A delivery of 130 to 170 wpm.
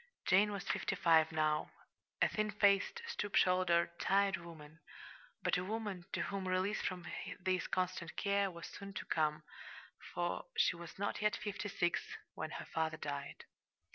Yes: average, 160 wpm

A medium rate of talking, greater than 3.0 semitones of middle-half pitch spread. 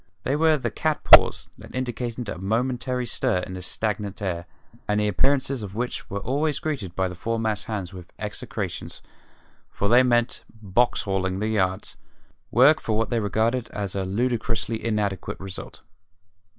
Yes: average, 165 wpm; average, 4.2 semitones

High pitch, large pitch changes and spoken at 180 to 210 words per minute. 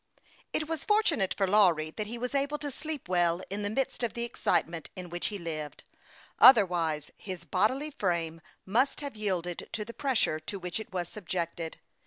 Yes: high, 195 Hz; wide, 6.2 semitones; average, 185 wpm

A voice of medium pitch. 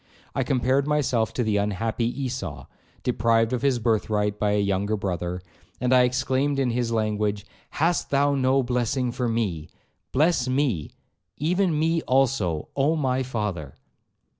No: low, 125 Hz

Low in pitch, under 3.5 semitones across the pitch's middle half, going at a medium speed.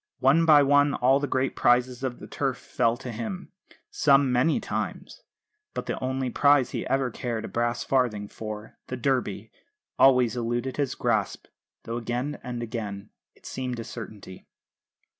Yes: low, 125 Hz; narrow, 2.6 semitones; average, 160 wpm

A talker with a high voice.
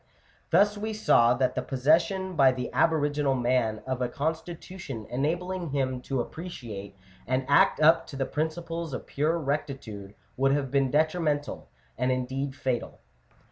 No: medium, 140 Hz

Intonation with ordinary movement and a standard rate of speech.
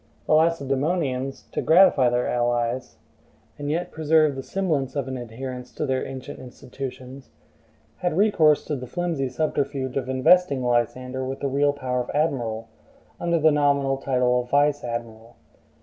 Yes: average, 3.2 semitones; average, 150 wpm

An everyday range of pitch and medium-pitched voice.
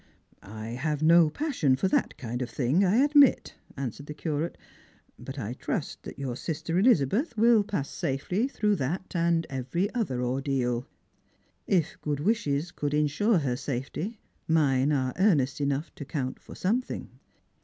No: wide, 6.2 semitones; medium, 150 Hz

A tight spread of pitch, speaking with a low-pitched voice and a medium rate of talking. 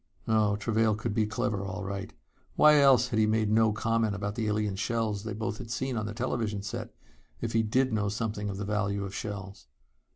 No: narrow, 1.7 semitones; low, 110 Hz; fast, 215 wpm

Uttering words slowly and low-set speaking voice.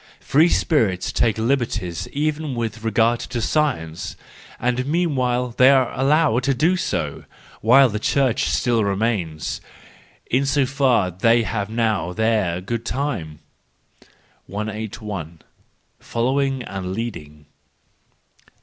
Yes: slow, 105 wpm; low, 115 Hz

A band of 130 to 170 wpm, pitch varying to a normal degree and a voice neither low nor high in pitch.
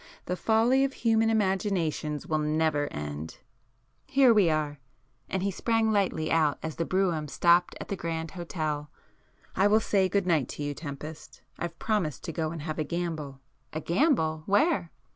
Yes: average, 160 wpm; average, 4.6 semitones; medium, 165 Hz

